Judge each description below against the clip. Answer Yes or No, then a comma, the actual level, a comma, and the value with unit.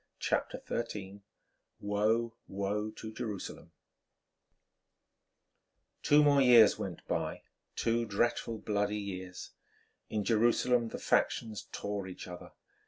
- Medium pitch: No, low, 105 Hz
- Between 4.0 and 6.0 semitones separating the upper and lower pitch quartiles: No, narrow, 2.5 semitones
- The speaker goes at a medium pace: No, slow, 100 wpm